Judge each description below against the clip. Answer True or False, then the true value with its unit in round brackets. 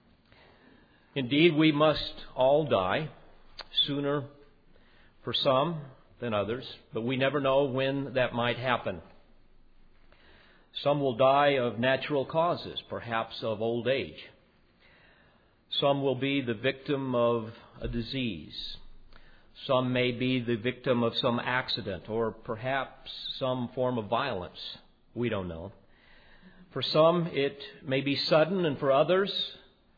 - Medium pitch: False (130 Hz)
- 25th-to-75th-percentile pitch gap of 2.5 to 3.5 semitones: True (3.0 semitones)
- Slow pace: True (125 wpm)